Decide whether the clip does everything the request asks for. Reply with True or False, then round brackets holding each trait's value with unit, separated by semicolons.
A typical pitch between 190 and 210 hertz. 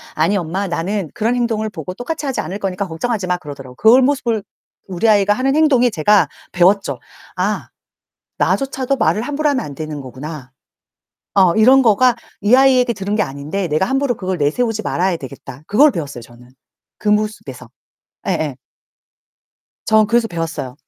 True (205 Hz)